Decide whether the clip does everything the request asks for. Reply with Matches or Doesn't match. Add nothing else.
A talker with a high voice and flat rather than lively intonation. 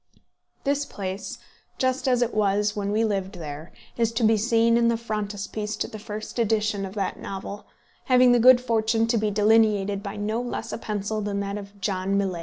Matches